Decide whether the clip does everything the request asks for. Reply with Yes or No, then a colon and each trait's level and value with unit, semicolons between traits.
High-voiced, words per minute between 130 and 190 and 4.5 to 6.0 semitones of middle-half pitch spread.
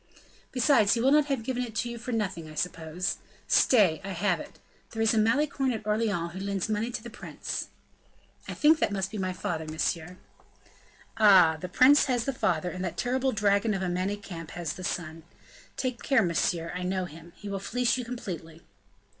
No: high, 200 Hz; average, 200 wpm; average, 5.2 semitones